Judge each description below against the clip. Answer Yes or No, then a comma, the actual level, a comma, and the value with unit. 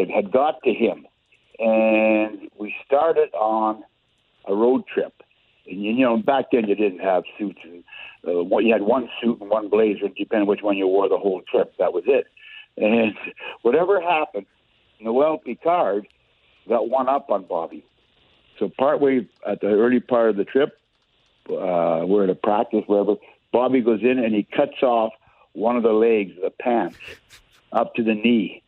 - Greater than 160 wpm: Yes, average, 175 wpm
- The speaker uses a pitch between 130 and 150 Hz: No, low, 110 Hz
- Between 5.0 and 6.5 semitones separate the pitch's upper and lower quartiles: Yes, wide, 5.6 semitones